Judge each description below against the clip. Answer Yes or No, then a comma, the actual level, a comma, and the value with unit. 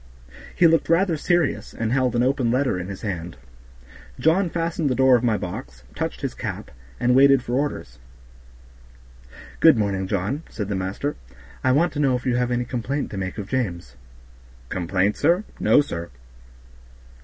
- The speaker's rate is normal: Yes, average, 170 wpm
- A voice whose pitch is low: Yes, low, 125 Hz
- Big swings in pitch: Yes, wide, 6.5 semitones